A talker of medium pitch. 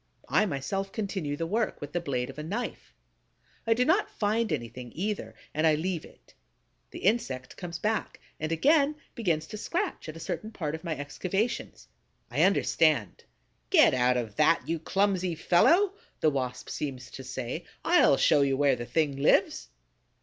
Yes: medium, 165 Hz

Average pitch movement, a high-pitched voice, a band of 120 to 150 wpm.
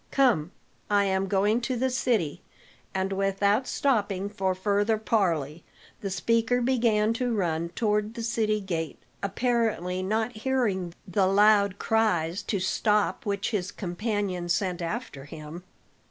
Yes: average, 3.4 semitones; high, 205 Hz; slow, 135 wpm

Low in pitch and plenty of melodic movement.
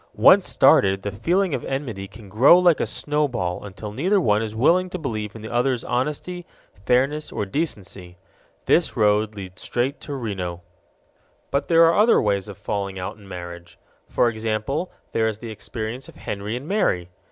Yes: low, 110 Hz; wide, 6.3 semitones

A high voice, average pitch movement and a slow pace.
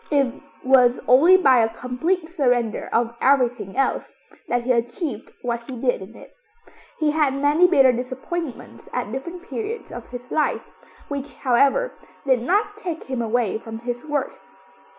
No: very high, 260 Hz; average, 4.2 semitones; average, 155 wpm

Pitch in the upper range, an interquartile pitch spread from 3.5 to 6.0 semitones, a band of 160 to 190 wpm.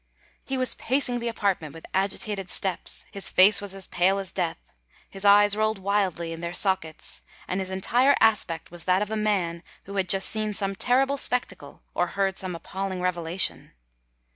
No: high, 195 Hz; average, 2.8 semitones; average, 170 wpm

